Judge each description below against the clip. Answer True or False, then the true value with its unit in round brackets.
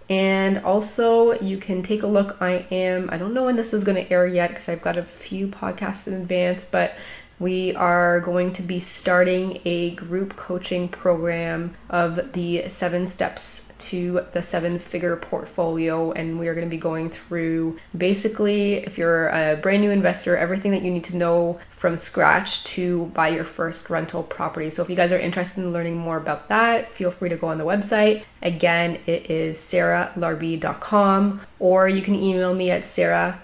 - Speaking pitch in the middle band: True (180 Hz)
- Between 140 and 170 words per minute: False (185 wpm)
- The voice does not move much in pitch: True (2.2 semitones)